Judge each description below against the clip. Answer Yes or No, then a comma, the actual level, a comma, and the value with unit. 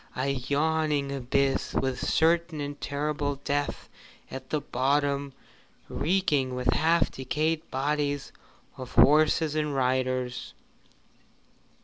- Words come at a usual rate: No, slow, 100 wpm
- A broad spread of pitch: No, narrow, 2.5 semitones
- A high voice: No, medium, 145 Hz